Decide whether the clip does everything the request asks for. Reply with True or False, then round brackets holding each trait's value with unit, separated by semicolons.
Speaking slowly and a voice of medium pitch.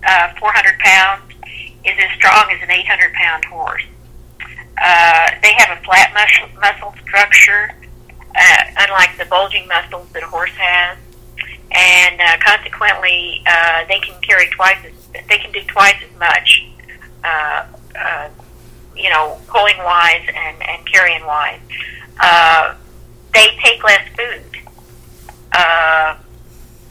True (130 wpm; 175 Hz)